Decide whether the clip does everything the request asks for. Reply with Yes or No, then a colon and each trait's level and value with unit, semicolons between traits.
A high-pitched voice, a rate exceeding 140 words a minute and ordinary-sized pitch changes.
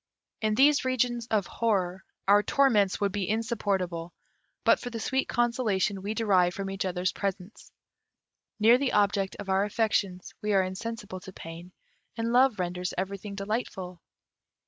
Yes: high, 205 Hz; average, 150 wpm; average, 3.4 semitones